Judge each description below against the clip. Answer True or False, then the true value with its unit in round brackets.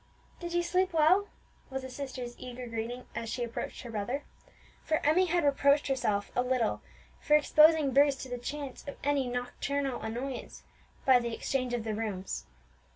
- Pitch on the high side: True (260 Hz)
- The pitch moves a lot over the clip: False (3.3 semitones)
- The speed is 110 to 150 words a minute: False (170 wpm)